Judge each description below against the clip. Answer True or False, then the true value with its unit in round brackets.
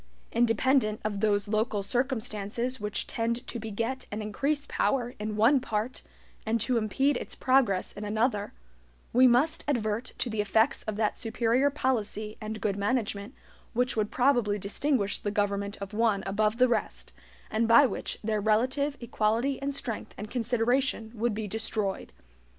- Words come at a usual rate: True (155 wpm)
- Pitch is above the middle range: True (225 Hz)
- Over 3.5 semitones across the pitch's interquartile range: False (3.2 semitones)